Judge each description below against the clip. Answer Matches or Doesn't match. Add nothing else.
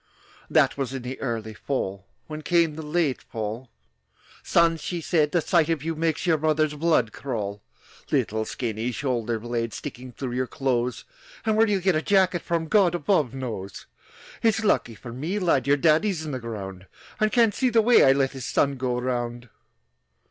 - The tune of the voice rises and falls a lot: Matches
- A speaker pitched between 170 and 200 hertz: Doesn't match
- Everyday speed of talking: Matches